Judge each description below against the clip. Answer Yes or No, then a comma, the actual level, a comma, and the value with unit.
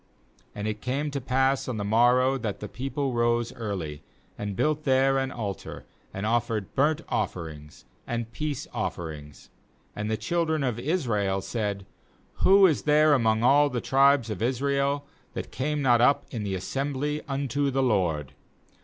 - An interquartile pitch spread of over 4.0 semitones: Yes, average, 5.0 semitones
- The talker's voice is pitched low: Yes, low, 125 Hz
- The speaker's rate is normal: Yes, average, 155 wpm